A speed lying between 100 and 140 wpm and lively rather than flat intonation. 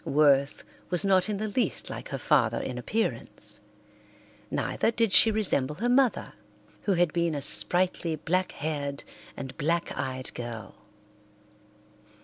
Yes: slow, 135 wpm; wide, 6.2 semitones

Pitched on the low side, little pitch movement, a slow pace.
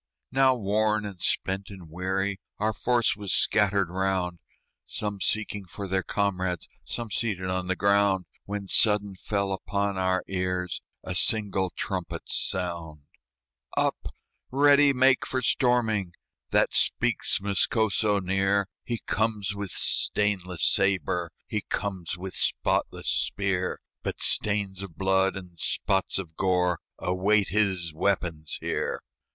Yes: very low, 95 Hz; narrow, 2.1 semitones; slow, 125 wpm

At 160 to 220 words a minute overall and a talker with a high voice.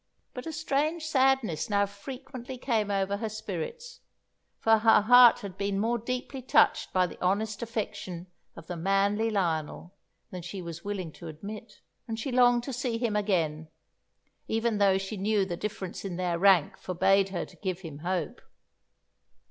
Yes: average, 165 wpm; high, 205 Hz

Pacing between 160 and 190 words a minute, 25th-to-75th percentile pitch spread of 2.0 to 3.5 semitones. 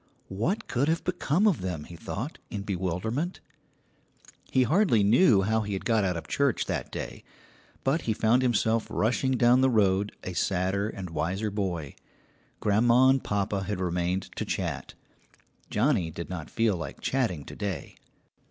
No: average, 165 wpm; wide, 5.4 semitones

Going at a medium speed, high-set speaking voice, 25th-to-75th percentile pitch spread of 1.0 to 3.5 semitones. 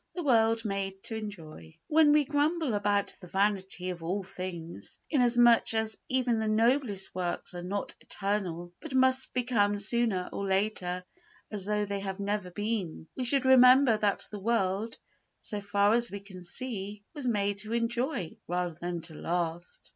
No: average, 170 wpm; high, 205 Hz; average, 4.1 semitones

